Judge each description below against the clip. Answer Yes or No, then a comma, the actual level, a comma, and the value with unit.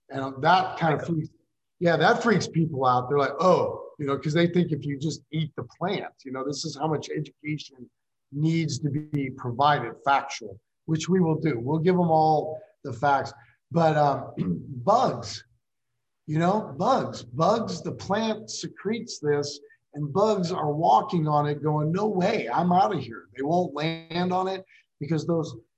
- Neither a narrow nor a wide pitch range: Yes, average, 3.7 semitones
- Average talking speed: Yes, average, 180 wpm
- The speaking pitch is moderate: Yes, medium, 155 Hz